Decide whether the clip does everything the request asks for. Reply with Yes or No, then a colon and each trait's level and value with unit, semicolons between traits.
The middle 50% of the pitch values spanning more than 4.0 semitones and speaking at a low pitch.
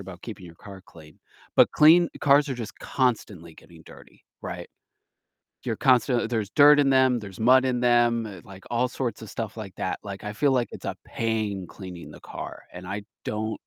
Yes: average, 4.6 semitones; low, 110 Hz